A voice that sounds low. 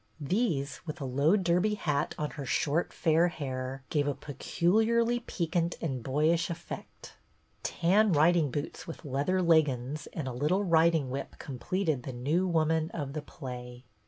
No: medium, 155 Hz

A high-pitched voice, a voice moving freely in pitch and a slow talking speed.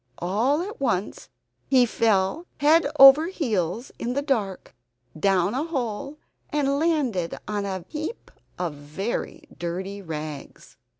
Yes: high, 225 Hz; wide, 7.3 semitones; slow, 125 wpm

